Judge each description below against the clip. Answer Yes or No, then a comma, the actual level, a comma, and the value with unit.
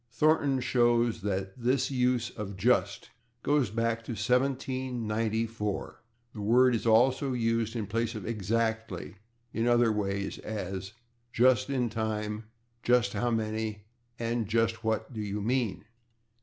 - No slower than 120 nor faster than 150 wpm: Yes, slow, 135 wpm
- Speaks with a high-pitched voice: No, low, 115 Hz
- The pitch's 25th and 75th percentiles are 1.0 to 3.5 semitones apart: Yes, narrow, 2.4 semitones